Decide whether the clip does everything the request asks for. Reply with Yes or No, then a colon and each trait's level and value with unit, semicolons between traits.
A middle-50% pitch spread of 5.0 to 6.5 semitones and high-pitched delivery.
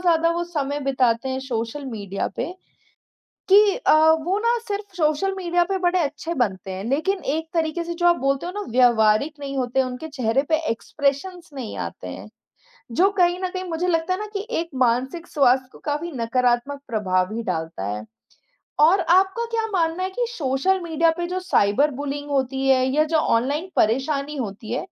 Yes: wide, 5.6 semitones; very high, 290 Hz